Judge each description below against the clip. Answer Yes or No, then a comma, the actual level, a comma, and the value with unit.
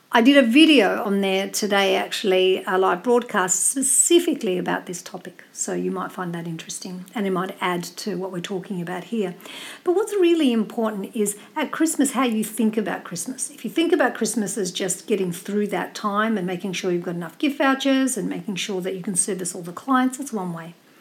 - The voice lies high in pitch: Yes, high, 205 Hz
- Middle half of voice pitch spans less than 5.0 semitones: No, wide, 5.4 semitones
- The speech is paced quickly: Yes, fast, 215 wpm